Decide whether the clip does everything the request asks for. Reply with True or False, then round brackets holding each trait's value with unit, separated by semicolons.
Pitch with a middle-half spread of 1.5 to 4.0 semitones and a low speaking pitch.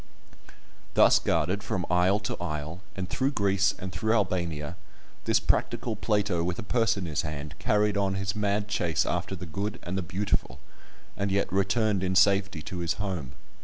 True (2.8 semitones; 95 Hz)